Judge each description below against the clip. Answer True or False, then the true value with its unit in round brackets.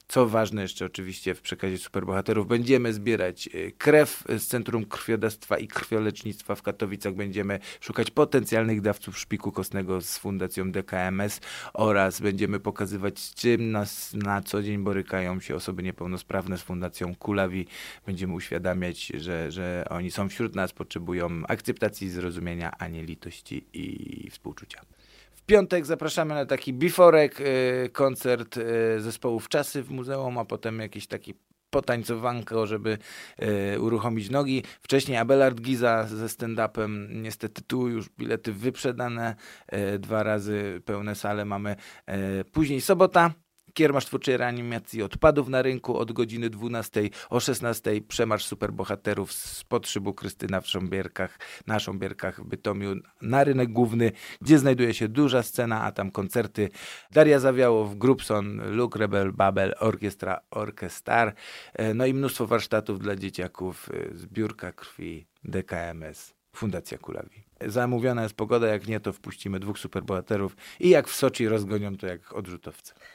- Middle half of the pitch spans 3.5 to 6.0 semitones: True (3.9 semitones)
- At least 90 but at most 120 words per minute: False (135 wpm)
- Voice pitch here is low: True (105 Hz)